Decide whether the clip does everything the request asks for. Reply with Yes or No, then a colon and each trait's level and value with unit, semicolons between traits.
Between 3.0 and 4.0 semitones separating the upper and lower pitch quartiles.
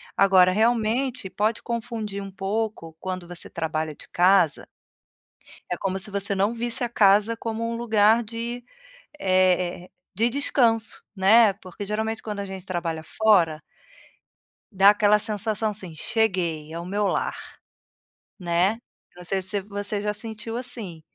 Yes: average, 3.3 semitones